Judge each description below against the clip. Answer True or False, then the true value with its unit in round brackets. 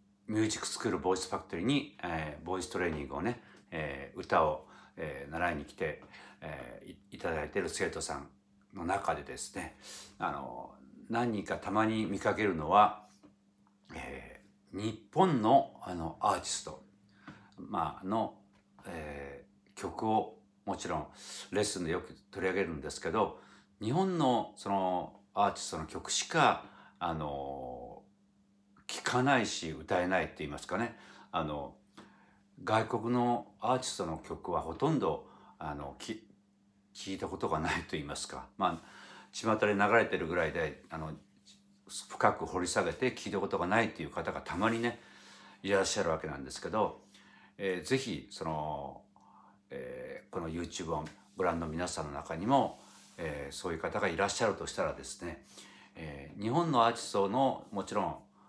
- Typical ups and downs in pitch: True (5.0 semitones)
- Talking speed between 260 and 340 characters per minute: True (295 characters per minute)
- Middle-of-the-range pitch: False (100 Hz)